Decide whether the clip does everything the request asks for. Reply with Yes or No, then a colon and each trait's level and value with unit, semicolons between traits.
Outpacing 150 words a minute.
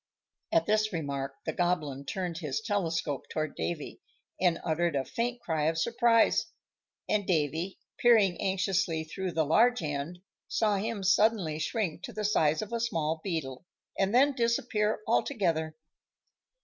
No: average, 145 wpm